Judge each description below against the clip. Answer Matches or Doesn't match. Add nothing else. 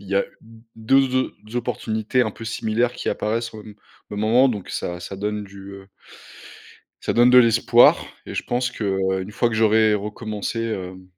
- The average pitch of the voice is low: Matches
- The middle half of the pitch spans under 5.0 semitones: Matches